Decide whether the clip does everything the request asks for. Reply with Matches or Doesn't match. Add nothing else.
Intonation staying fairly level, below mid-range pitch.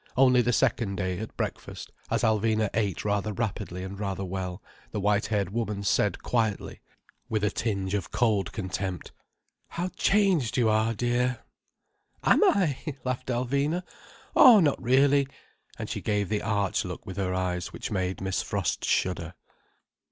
Doesn't match